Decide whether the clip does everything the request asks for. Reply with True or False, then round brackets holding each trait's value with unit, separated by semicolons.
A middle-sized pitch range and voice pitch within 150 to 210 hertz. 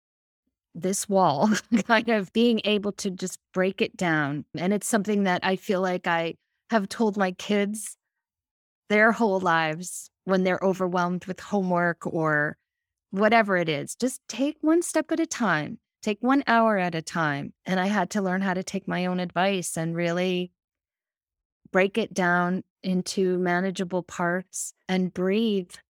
True (3.0 semitones; 185 Hz)